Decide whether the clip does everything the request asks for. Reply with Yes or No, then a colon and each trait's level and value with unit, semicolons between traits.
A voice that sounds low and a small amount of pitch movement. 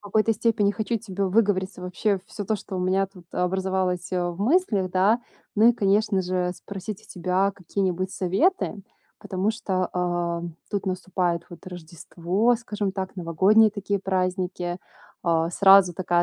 No: high, 190 Hz; narrow, 2.3 semitones